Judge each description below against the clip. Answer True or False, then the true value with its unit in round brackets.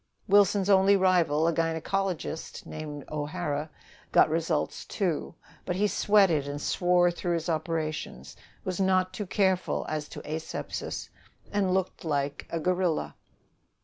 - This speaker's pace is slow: True (130 wpm)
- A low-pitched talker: False (175 Hz)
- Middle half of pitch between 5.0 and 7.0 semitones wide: False (3.4 semitones)